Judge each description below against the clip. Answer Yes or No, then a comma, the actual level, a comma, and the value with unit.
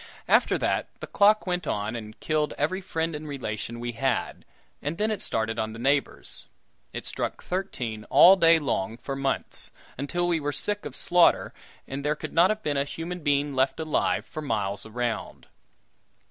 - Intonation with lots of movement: Yes, wide, 6.0 semitones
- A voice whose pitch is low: No, medium, 145 Hz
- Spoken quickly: No, average, 180 wpm